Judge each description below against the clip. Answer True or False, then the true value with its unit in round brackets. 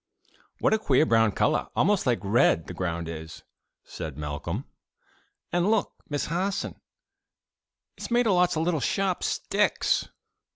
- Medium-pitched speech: True (155 Hz)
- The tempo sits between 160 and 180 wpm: False (150 wpm)